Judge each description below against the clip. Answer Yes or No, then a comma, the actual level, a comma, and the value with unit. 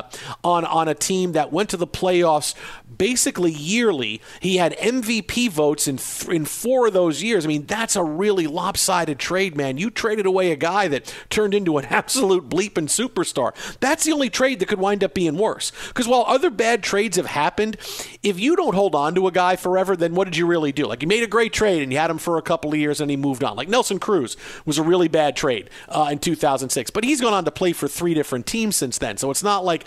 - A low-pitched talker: No, medium, 180 Hz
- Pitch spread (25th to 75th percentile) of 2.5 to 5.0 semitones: No, wide, 5.6 semitones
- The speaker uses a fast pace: Yes, fast, 240 wpm